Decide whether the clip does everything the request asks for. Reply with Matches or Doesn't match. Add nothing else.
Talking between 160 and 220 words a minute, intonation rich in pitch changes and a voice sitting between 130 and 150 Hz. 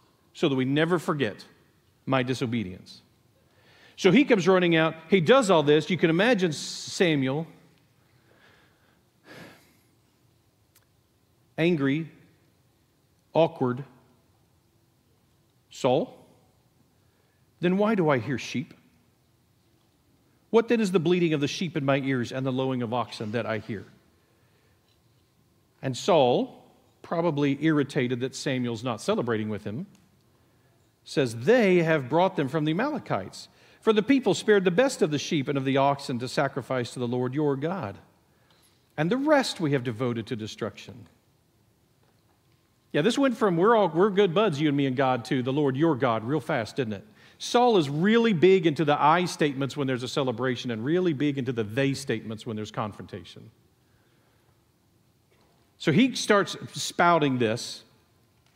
Doesn't match